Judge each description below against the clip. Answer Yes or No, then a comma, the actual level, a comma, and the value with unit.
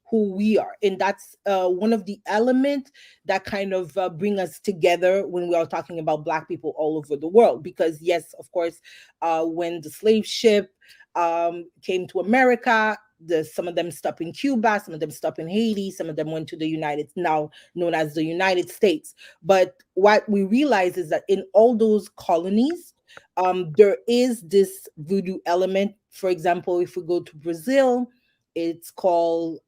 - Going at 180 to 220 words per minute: Yes, average, 185 wpm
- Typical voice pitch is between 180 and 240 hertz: Yes, medium, 185 Hz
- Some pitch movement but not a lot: Yes, average, 3.9 semitones